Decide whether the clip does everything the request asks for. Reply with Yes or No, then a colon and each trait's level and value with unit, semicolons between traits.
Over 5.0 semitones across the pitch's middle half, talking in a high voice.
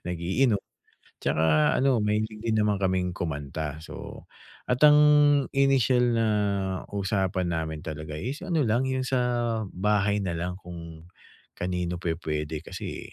No: wide, 5.6 semitones; very low, 95 Hz